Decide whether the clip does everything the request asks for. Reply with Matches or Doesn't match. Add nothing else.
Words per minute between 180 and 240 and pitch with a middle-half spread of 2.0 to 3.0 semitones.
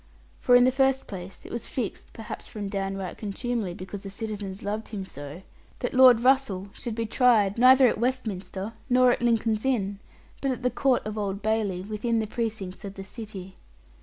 Doesn't match